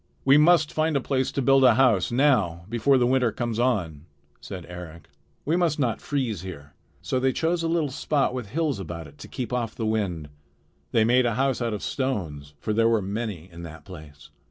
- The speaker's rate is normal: No, fast, 210 wpm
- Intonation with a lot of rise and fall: Yes, wide, 7.2 semitones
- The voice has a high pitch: No, low, 115 Hz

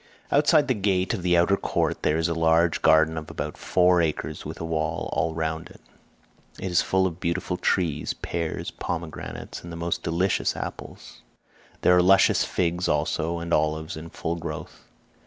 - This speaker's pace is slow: No, average, 175 wpm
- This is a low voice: Yes, very low, 85 Hz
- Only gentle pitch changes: Yes, narrow, 1.9 semitones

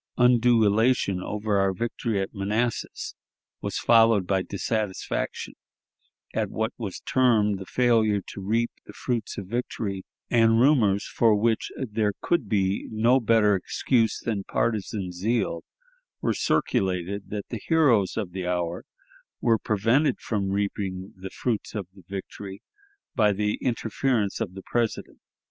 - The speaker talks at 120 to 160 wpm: Yes, average, 140 wpm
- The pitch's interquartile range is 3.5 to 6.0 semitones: No, average, 3.1 semitones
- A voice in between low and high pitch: No, low, 105 Hz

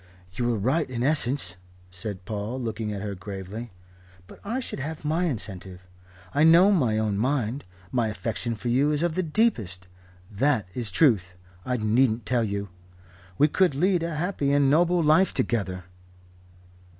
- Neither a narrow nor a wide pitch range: No, wide, 6.5 semitones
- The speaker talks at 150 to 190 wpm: Yes, average, 160 wpm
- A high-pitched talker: No, low, 120 Hz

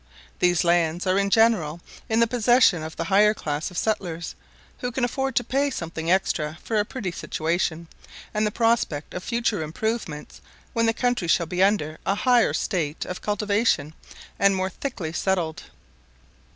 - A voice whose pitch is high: Yes, high, 195 Hz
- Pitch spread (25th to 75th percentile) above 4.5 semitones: Yes, average, 5.3 semitones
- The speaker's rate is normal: Yes, average, 165 wpm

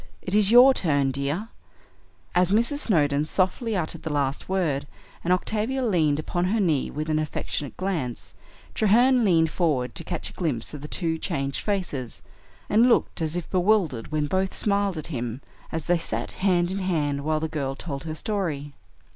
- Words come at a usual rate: Yes, average, 180 wpm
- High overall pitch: No, medium, 165 Hz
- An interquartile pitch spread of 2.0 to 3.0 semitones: No, average, 5.1 semitones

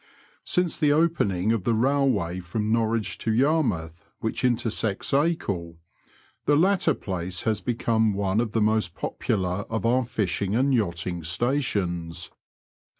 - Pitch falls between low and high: No, low, 110 Hz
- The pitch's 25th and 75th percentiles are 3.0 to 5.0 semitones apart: No, wide, 5.6 semitones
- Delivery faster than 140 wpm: No, slow, 135 wpm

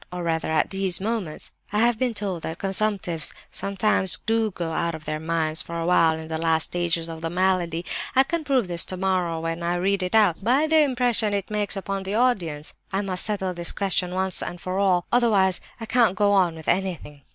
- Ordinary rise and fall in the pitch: Yes, average, 3.7 semitones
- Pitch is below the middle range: No, medium, 185 Hz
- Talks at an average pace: No, fast, 215 wpm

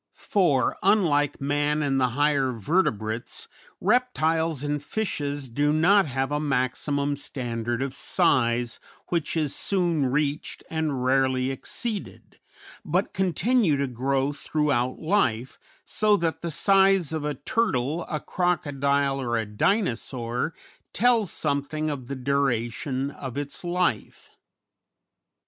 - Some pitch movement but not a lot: Yes, average, 4.1 semitones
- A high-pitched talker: No, medium, 145 Hz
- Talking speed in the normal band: No, slow, 120 wpm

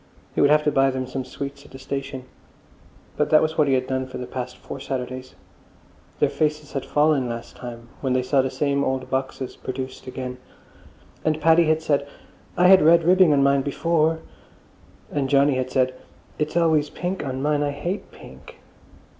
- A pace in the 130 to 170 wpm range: No, average, 195 wpm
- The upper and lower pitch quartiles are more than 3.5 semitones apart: No, average, 2.8 semitones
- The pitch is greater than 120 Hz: Yes, medium, 140 Hz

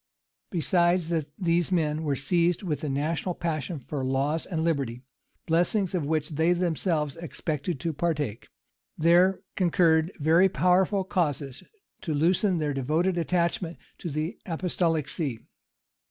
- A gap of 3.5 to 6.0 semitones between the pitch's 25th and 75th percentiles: No, average, 2.8 semitones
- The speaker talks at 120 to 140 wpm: Yes, slow, 135 wpm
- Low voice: No, medium, 165 Hz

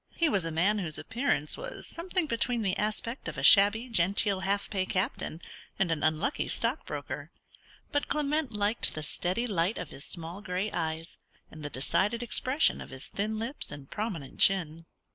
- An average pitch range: No, wide, 6.0 semitones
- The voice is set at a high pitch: Yes, high, 200 Hz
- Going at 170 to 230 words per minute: Yes, average, 175 wpm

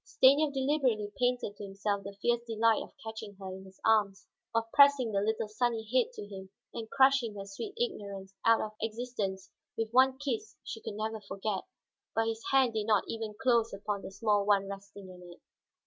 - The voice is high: Yes, high, 220 Hz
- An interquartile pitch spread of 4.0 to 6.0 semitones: No, average, 3.3 semitones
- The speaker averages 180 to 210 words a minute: Yes, average, 195 wpm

